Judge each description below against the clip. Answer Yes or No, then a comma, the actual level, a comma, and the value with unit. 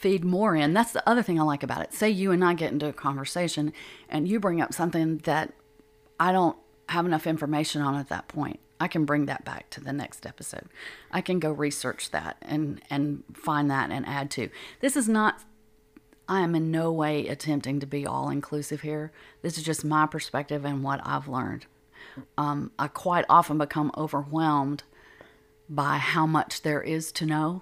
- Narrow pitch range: Yes, narrow, 2.3 semitones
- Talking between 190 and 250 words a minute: Yes, average, 200 wpm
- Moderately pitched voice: Yes, medium, 150 Hz